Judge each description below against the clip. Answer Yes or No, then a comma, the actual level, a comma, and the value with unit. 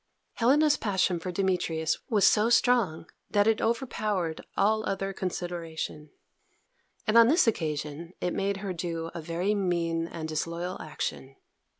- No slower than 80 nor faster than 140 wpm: Yes, slow, 135 wpm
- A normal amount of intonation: Yes, average, 4.4 semitones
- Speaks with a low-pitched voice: No, medium, 180 Hz